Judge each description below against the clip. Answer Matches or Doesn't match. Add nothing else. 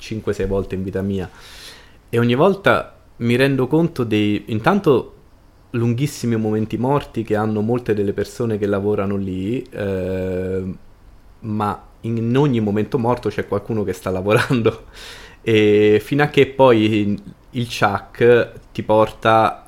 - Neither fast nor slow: Matches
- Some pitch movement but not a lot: Matches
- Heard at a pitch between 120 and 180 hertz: Doesn't match